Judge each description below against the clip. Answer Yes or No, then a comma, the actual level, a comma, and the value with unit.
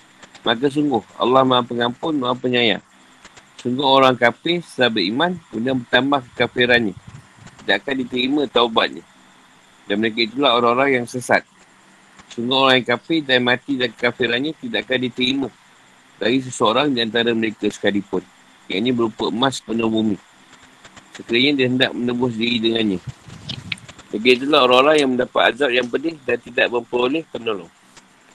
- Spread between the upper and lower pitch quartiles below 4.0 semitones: Yes, narrow, 2.4 semitones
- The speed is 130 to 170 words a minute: Yes, average, 140 wpm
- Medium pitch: No, low, 125 Hz